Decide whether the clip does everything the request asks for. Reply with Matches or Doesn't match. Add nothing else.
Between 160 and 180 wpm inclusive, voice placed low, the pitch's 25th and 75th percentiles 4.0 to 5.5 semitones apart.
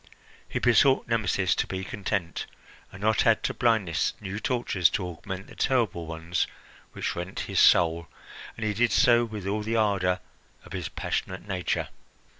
Doesn't match